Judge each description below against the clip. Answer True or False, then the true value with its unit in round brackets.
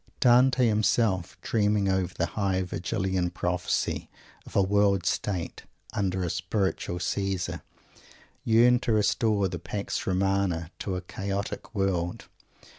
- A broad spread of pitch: False (2.6 semitones)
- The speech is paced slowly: True (120 wpm)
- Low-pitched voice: True (95 Hz)